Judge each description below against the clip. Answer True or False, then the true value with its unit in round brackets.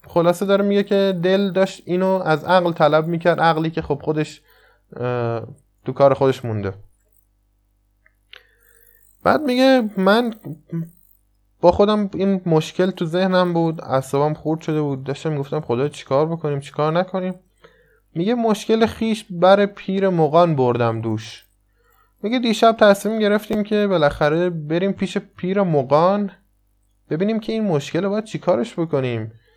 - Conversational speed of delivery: True (135 wpm)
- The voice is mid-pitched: True (165 Hz)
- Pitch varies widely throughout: True (6.1 semitones)